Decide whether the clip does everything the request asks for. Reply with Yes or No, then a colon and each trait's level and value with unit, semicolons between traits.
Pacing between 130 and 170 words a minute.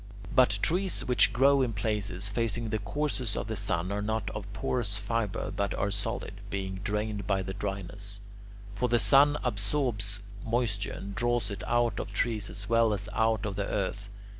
No: average, 180 wpm